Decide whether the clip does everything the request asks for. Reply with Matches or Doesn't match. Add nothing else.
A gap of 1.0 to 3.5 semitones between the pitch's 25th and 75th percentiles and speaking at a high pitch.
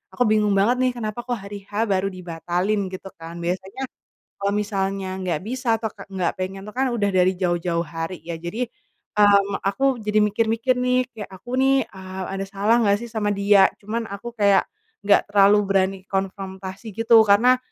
Matches